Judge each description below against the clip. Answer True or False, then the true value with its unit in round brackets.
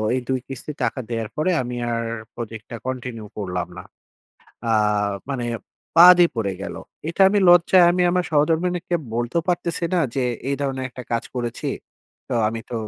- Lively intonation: True (6.5 semitones)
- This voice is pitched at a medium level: False (130 Hz)